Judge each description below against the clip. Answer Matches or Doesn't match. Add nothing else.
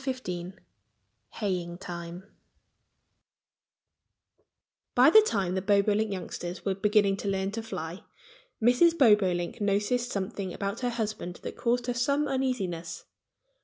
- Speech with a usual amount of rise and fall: Matches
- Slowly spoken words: Matches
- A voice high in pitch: Matches